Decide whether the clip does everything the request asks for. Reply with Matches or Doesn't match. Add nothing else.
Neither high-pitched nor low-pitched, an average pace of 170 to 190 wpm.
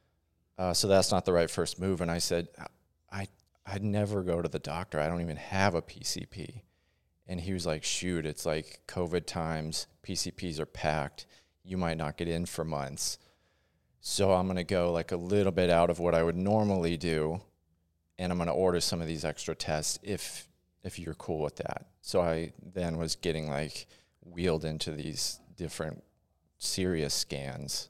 Doesn't match